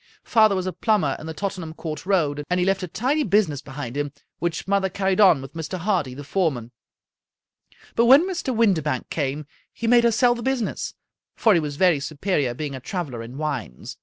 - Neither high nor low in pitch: Yes, medium, 175 Hz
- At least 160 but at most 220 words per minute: Yes, average, 200 wpm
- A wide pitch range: Yes, wide, 6.0 semitones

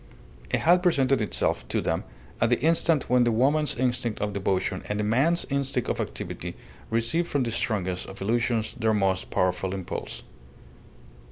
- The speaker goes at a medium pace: Yes, average, 165 wpm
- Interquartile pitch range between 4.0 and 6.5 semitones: Yes, average, 4.8 semitones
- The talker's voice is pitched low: Yes, low, 115 Hz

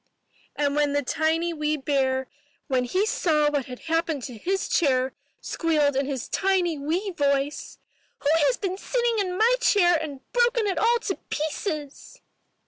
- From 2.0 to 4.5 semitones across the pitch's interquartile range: No, average, 5.0 semitones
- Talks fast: No, average, 160 wpm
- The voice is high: Yes, very high, 310 Hz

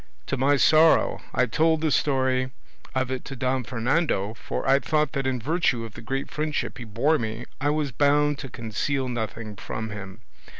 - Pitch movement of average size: Yes, average, 4.2 semitones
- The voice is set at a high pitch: No, low, 130 Hz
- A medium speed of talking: Yes, average, 185 wpm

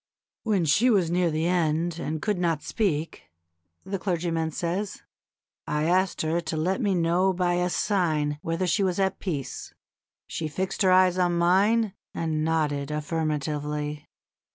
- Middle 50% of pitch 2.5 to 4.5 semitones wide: Yes, average, 3.0 semitones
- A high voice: No, medium, 170 Hz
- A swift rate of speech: No, average, 155 wpm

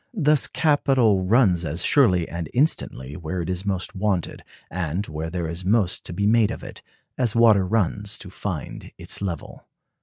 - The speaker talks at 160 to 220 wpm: Yes, average, 175 wpm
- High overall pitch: No, very low, 95 Hz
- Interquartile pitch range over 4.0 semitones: Yes, average, 4.6 semitones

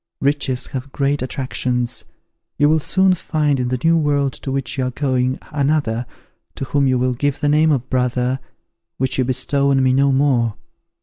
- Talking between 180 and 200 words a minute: Yes, average, 185 wpm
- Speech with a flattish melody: Yes, narrow, 2.2 semitones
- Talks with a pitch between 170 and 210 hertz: No, low, 135 Hz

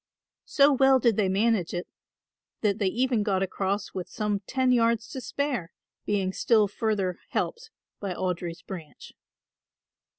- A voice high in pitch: Yes, high, 210 Hz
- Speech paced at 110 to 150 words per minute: Yes, average, 140 wpm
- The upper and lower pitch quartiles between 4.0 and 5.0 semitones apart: Yes, average, 4.4 semitones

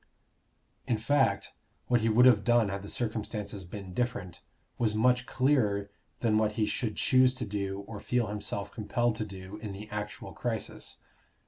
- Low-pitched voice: Yes, low, 110 Hz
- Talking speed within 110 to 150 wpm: No, average, 165 wpm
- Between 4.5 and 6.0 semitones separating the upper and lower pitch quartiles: No, average, 3.0 semitones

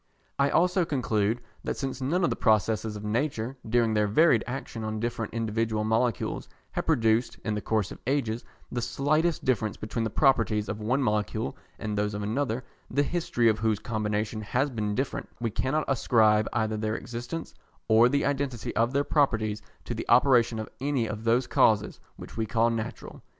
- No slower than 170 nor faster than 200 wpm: Yes, average, 180 wpm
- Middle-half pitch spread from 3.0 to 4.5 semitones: Yes, average, 3.4 semitones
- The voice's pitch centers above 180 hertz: No, low, 115 Hz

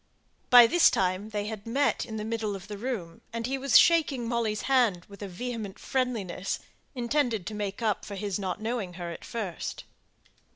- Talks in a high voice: Yes, high, 215 Hz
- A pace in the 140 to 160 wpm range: No, average, 180 wpm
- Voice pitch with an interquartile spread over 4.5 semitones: No, average, 3.7 semitones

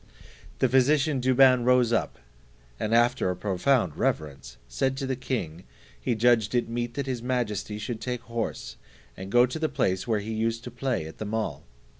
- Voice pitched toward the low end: Yes, low, 120 Hz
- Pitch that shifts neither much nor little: Yes, average, 3.4 semitones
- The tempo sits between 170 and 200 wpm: Yes, average, 180 wpm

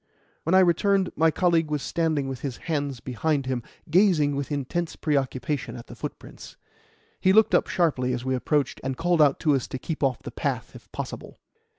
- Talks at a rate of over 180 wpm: Yes, average, 195 wpm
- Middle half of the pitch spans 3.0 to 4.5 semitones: Yes, average, 4.0 semitones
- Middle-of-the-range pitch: Yes, medium, 150 Hz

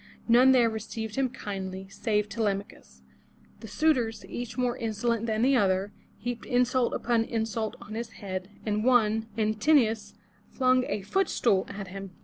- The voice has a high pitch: Yes, high, 225 Hz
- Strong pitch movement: No, average, 3.0 semitones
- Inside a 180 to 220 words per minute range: No, average, 170 wpm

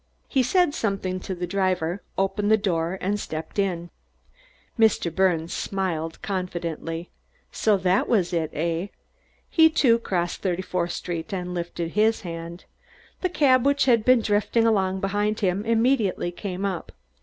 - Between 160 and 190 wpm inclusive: No, average, 150 wpm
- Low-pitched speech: No, high, 190 Hz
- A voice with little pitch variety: No, average, 3.8 semitones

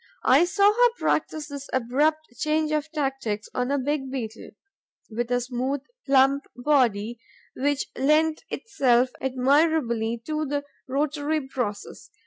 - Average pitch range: Yes, average, 3.5 semitones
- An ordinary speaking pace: No, slow, 125 wpm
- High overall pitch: Yes, very high, 275 Hz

